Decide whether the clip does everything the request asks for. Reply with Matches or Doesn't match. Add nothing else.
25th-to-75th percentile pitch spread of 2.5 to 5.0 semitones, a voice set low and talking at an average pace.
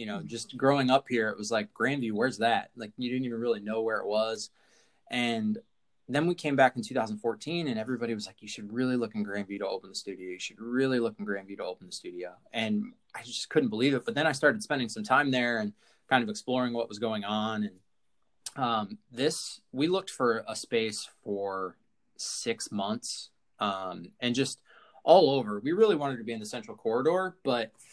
Doesn't match